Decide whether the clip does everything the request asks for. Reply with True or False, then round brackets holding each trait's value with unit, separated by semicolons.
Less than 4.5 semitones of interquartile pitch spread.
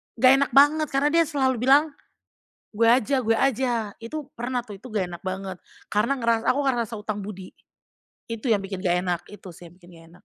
False (5.4 semitones)